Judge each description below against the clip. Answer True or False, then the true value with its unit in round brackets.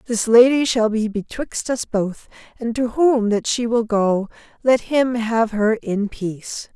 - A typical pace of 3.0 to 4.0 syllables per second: True (3.9 syllables/s)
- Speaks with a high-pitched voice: True (225 Hz)